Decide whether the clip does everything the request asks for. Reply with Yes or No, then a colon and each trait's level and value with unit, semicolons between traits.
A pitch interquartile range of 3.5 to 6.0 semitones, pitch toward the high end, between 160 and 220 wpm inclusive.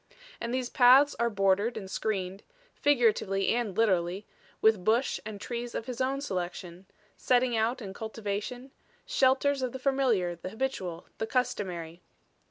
No: average, 4.8 semitones; high, 220 Hz; average, 145 wpm